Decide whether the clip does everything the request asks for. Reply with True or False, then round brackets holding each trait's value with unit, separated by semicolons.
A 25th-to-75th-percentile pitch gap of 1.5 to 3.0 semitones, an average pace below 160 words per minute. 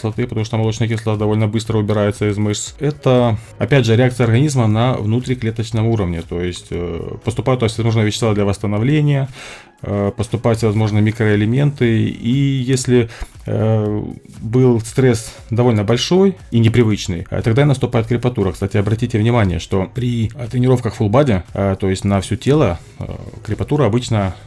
True (2.7 semitones; 140 wpm)